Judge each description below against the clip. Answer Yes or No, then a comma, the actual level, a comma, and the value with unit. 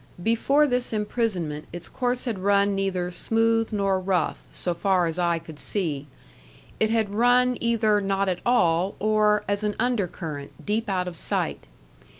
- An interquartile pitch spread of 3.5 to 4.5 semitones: Yes, average, 4.0 semitones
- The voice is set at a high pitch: Yes, high, 200 Hz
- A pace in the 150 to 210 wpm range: Yes, average, 155 wpm